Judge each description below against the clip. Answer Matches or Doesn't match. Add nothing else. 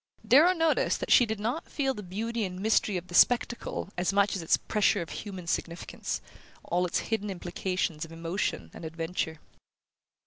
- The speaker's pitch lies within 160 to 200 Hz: Matches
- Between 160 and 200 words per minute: Matches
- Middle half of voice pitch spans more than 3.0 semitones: Matches